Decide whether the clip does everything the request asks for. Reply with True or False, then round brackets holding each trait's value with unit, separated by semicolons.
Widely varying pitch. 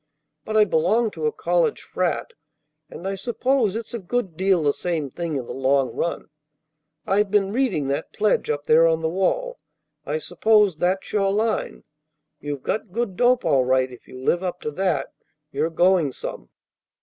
True (6.0 semitones)